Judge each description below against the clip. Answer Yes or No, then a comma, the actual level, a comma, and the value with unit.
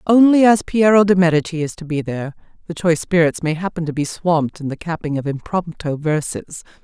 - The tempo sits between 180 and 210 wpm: Yes, average, 200 wpm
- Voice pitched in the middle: Yes, medium, 165 Hz